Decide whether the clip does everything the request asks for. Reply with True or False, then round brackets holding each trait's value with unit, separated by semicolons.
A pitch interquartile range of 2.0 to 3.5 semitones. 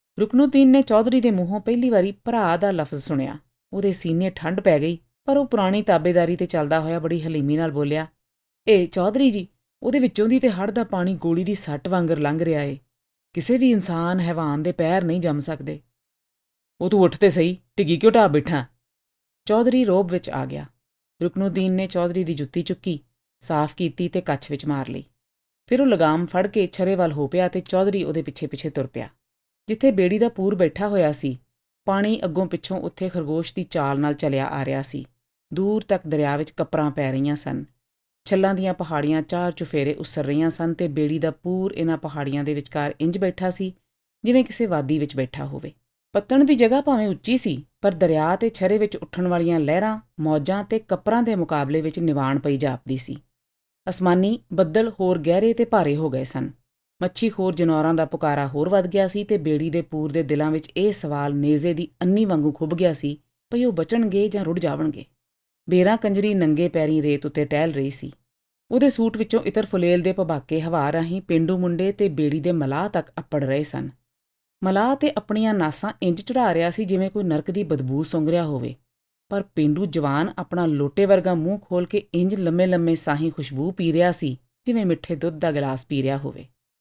False (4.7 semitones)